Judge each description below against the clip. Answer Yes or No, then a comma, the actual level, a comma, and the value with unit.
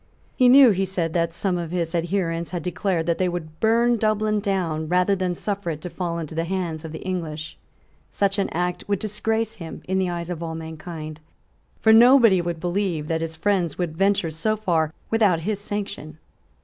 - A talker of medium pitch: Yes, medium, 180 Hz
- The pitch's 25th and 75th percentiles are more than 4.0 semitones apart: No, average, 3.6 semitones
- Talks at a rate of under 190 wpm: No, average, 200 wpm